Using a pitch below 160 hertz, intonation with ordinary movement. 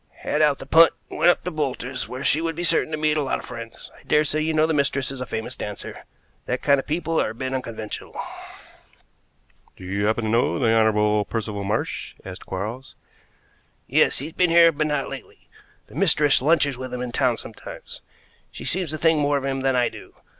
Yes: low, 135 Hz; average, 4.9 semitones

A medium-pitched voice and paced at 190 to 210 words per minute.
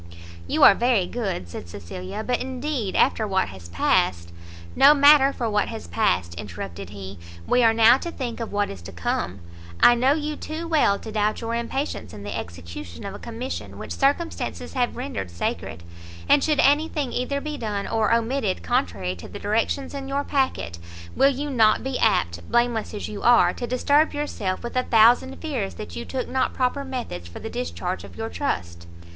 No: high, 230 Hz; average, 195 wpm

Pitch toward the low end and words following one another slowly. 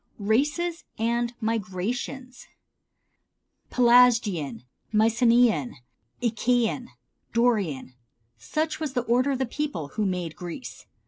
No: high, 235 Hz; slow, 90 wpm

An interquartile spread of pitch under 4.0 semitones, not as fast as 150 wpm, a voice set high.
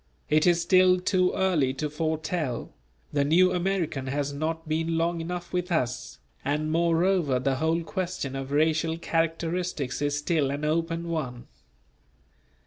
No: average, 3.1 semitones; average, 140 wpm; medium, 160 Hz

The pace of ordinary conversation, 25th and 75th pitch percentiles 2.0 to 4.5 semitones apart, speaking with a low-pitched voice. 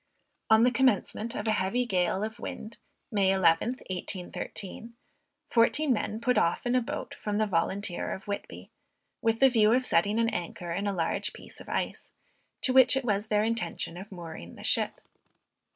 No: average, 180 wpm; average, 3.7 semitones; high, 210 Hz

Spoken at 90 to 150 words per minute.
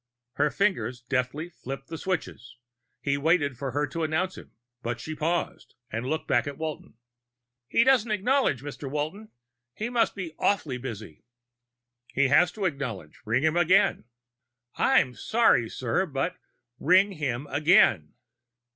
Yes: average, 145 wpm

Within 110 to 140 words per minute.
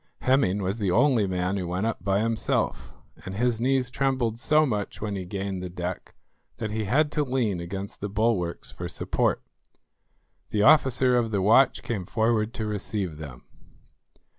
No: average, 170 wpm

